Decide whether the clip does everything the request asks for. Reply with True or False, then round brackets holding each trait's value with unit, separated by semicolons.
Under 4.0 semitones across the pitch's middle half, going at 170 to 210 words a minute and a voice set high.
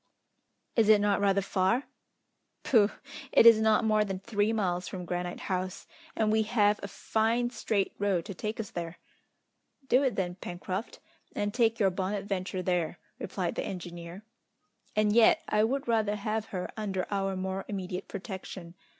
False (2.8 semitones; 160 wpm; 200 Hz)